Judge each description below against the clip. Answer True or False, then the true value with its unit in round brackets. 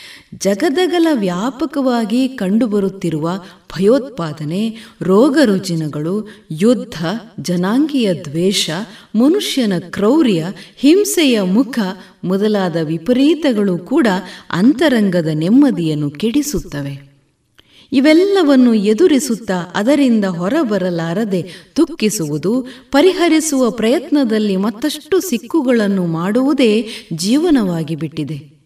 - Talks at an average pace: False (60 wpm)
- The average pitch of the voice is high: True (215 Hz)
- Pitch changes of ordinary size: False (7.0 semitones)